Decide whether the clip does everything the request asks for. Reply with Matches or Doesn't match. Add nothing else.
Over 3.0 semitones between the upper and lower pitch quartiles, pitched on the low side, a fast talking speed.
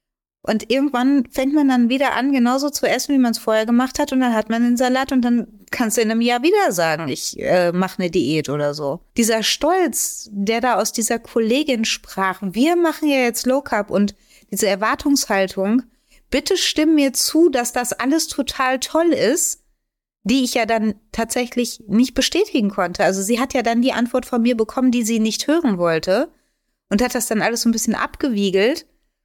Doesn't match